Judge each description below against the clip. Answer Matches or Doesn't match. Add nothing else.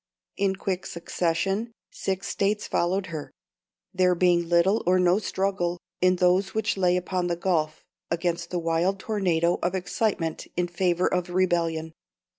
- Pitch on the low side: Doesn't match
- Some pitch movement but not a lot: Doesn't match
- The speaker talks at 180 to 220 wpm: Doesn't match